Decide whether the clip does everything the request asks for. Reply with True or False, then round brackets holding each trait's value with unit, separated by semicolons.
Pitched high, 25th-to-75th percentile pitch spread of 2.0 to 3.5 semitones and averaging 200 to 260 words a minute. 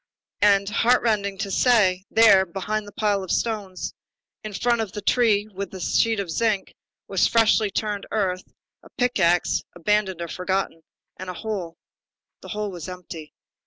False (200 Hz; 2.6 semitones; 160 wpm)